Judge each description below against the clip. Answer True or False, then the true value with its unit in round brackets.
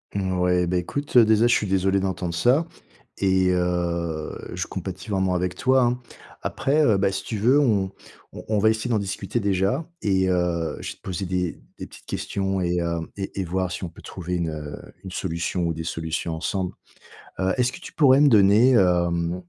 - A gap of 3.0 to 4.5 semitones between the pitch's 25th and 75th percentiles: True (3.3 semitones)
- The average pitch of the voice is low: True (95 Hz)